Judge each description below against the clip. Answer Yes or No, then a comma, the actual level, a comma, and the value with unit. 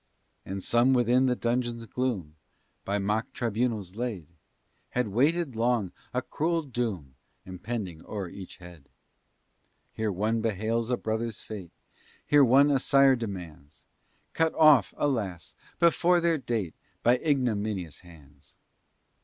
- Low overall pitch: Yes, low, 115 Hz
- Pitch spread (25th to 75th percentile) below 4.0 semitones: No, average, 4.7 semitones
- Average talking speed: No, slow, 125 wpm